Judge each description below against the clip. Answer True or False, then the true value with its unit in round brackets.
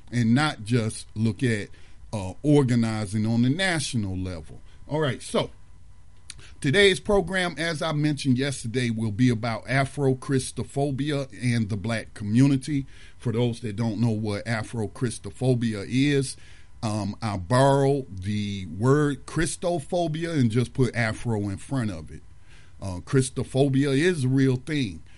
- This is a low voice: True (120 Hz)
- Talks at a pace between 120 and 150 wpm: True (135 wpm)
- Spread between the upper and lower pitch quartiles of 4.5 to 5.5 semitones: True (4.8 semitones)